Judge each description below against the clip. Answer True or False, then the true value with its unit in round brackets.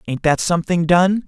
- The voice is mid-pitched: True (170 Hz)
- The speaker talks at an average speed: True (190 wpm)